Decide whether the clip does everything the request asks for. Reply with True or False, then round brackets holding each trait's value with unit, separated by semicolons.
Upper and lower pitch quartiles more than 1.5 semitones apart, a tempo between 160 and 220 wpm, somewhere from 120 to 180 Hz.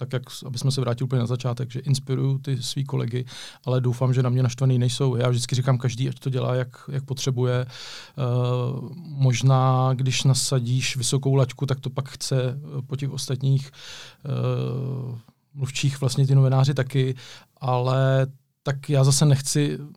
False (1.2 semitones; 165 wpm; 130 Hz)